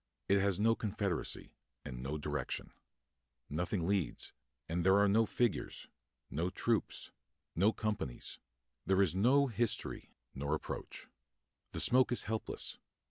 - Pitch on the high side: No, low, 100 Hz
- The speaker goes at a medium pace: No, slow, 130 wpm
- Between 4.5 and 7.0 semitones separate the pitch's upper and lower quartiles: Yes, average, 5.0 semitones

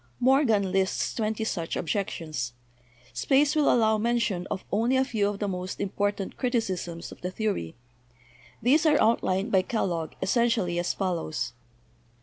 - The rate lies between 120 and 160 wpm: Yes, average, 140 wpm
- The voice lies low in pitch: No, high, 205 Hz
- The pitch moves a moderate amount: Yes, average, 4.5 semitones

